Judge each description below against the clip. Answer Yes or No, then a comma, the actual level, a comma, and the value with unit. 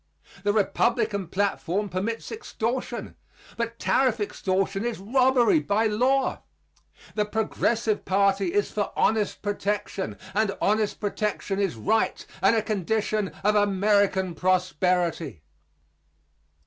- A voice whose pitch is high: Yes, high, 205 Hz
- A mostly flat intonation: Yes, narrow, 2.3 semitones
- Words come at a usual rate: No, slow, 110 wpm